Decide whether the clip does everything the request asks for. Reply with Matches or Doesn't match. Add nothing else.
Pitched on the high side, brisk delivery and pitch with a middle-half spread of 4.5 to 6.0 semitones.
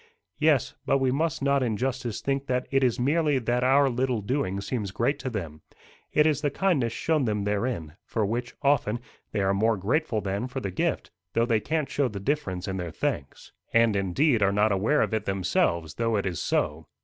Doesn't match